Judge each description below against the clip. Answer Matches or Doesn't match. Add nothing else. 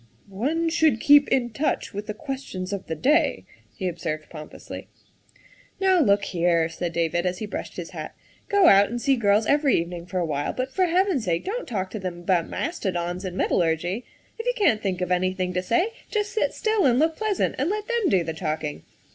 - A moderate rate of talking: Doesn't match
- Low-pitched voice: Doesn't match